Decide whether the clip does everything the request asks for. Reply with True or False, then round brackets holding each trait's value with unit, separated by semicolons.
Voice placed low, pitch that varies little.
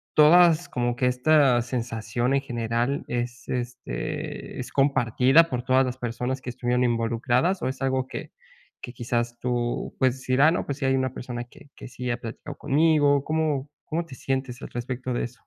True (125 Hz; 2.3 semitones)